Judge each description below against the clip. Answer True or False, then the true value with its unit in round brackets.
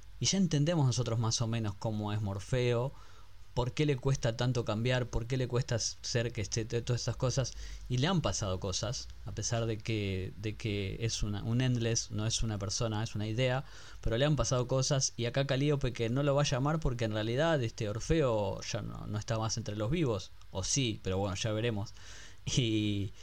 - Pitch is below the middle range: True (115 Hz)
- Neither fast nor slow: False (210 wpm)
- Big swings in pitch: False (3.4 semitones)